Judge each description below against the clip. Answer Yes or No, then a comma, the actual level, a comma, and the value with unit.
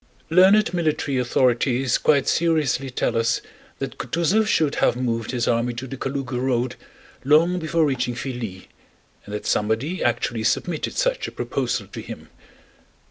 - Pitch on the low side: Yes, low, 130 Hz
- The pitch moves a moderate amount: Yes, average, 4.9 semitones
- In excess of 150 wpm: No, average, 145 wpm